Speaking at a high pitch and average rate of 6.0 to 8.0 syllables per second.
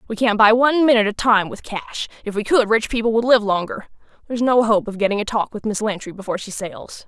Yes: high, 215 Hz; 6.3 syllables/s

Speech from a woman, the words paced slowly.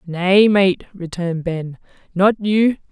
Yes: female; slow, 125 wpm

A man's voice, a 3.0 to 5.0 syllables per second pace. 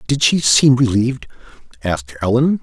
No: male; 5.4 syllables/s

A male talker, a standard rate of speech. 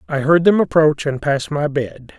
No: male; fast, 220 wpm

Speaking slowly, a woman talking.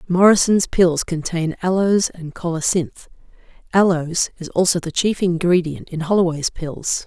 Yes: slow, 125 wpm; female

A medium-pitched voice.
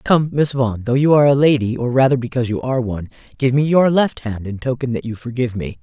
No: low, 125 Hz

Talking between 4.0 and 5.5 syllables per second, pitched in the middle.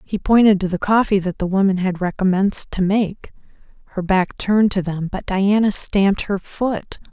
No: 4.9 syllables/s; high, 195 Hz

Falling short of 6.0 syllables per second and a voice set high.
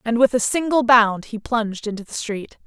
Yes: 5.2 syllables/s; high, 230 Hz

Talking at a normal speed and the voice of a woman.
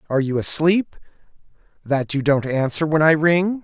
No: average, 165 wpm; male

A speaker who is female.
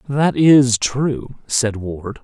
No: male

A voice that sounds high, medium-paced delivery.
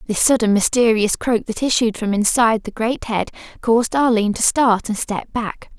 Yes: high, 225 Hz; average, 185 wpm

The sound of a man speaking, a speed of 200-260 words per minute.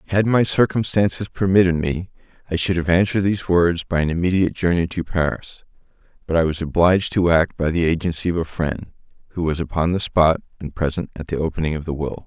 Yes: male; fast, 205 wpm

